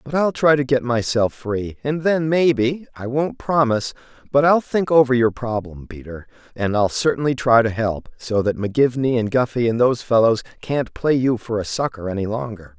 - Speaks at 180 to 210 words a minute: Yes, average, 190 wpm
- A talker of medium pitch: No, low, 125 Hz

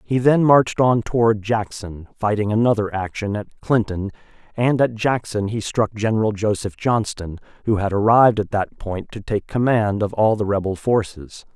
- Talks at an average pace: Yes, average, 170 wpm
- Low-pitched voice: Yes, low, 110 Hz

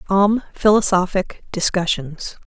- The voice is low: No, high, 190 Hz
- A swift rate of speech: No, slow, 75 wpm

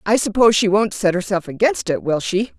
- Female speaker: Yes, female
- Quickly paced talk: Yes, fast, 230 wpm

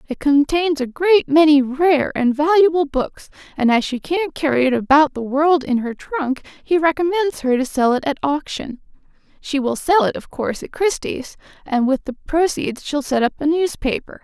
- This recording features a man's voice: No, female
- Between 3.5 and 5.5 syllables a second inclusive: Yes, 4.7 syllables/s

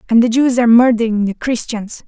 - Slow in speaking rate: No, fast, 205 wpm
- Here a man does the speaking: No, female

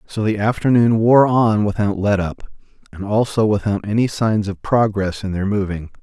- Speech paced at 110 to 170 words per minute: Yes, average, 160 wpm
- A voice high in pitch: No, low, 105 Hz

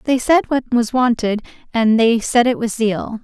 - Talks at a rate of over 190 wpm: Yes, fast, 205 wpm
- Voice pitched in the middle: No, high, 235 Hz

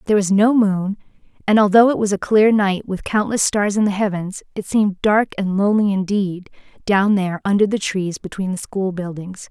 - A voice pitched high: Yes, high, 200 Hz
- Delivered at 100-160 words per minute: No, average, 200 wpm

